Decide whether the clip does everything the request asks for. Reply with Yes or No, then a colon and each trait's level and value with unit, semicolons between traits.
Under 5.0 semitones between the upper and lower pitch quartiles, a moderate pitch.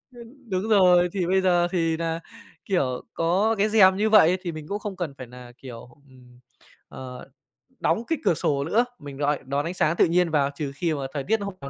No: average, 5.3 semitones; medium, 170 Hz